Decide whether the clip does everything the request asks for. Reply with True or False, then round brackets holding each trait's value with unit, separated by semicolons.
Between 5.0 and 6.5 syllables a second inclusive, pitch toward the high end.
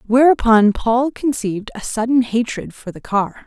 False (4.6 syllables/s; 235 Hz)